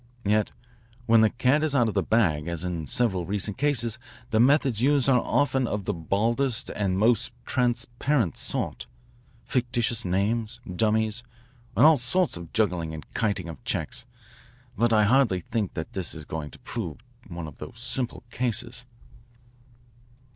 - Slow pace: No, average, 155 wpm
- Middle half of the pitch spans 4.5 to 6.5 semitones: Yes, average, 4.9 semitones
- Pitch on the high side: No, low, 110 Hz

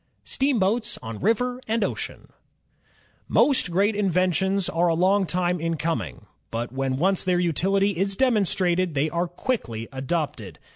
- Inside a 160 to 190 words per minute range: No, average, 140 wpm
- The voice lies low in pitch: No, medium, 180 Hz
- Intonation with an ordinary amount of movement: Yes, average, 3.8 semitones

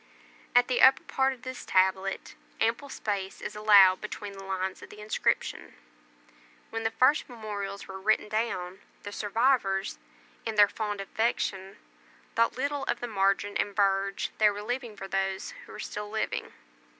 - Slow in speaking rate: No, average, 160 wpm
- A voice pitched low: No, high, 210 Hz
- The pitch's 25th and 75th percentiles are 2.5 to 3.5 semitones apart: Yes, average, 2.9 semitones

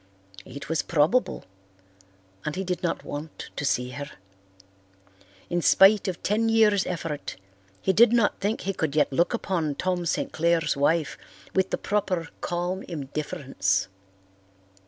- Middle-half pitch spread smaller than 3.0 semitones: No, average, 4.4 semitones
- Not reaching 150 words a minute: Yes, average, 140 wpm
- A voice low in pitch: No, medium, 170 Hz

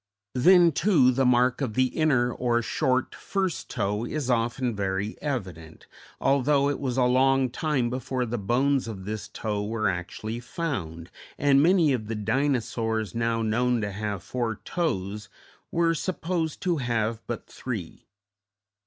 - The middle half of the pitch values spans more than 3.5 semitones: Yes, average, 4.2 semitones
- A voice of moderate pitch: No, low, 125 Hz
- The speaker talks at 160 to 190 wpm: No, average, 150 wpm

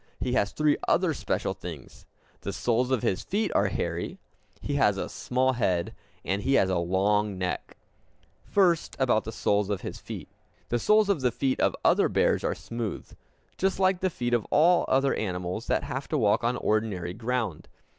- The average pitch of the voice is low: Yes, low, 115 Hz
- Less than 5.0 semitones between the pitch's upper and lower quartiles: No, wide, 5.5 semitones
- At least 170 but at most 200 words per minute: Yes, average, 185 wpm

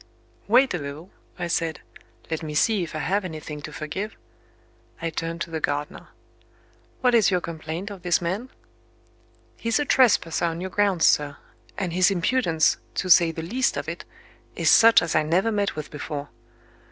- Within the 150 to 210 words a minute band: Yes, average, 175 wpm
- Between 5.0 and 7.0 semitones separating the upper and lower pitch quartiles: No, average, 4.2 semitones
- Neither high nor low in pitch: Yes, medium, 170 Hz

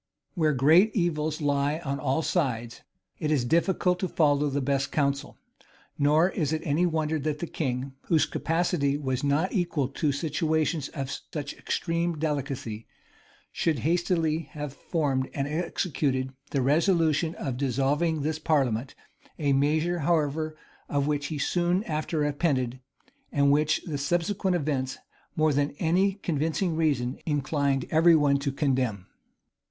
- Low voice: No, medium, 150 Hz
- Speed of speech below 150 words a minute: Yes, average, 140 wpm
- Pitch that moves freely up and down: No, average, 2.7 semitones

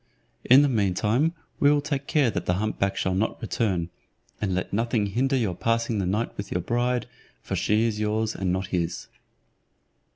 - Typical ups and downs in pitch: Yes, average, 4.2 semitones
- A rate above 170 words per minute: Yes, average, 195 wpm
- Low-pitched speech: Yes, low, 110 Hz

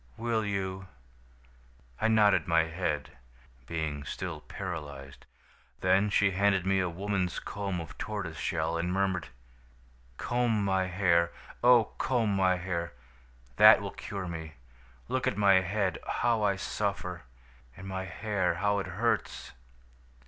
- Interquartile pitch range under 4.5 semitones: Yes, average, 2.9 semitones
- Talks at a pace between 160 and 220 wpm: No, slow, 135 wpm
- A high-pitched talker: No, very low, 95 Hz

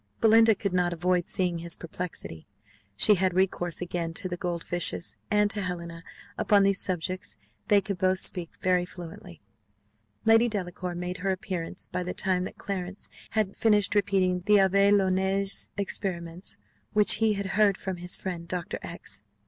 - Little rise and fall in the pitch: Yes, narrow, 2.2 semitones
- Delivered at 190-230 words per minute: No, average, 165 wpm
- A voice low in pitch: No, medium, 185 Hz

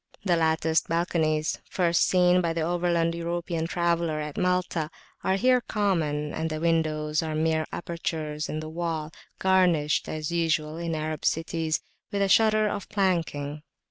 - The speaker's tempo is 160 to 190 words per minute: No, average, 150 wpm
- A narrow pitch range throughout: Yes, narrow, 2.1 semitones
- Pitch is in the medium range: Yes, medium, 165 Hz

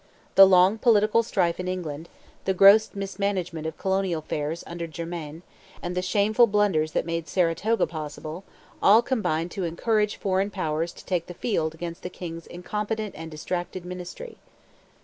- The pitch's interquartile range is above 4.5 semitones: No, average, 3.5 semitones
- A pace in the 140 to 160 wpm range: Yes, average, 155 wpm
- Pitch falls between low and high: Yes, medium, 180 Hz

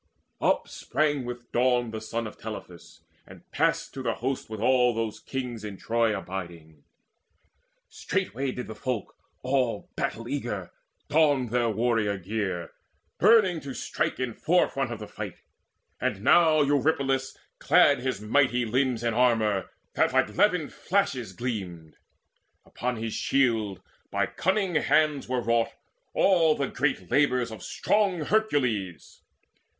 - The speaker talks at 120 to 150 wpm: Yes, average, 140 wpm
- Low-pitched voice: Yes, low, 125 Hz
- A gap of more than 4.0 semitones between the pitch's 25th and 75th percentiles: Yes, average, 4.5 semitones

